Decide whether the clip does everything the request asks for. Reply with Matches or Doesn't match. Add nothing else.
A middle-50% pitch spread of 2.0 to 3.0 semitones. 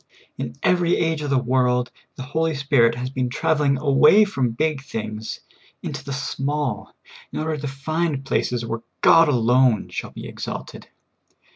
Doesn't match